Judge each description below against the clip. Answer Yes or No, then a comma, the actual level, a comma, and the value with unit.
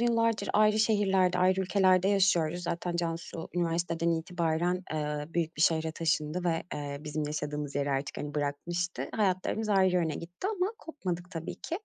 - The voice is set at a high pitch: No, medium, 175 Hz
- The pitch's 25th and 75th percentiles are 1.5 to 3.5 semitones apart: Yes, average, 3.2 semitones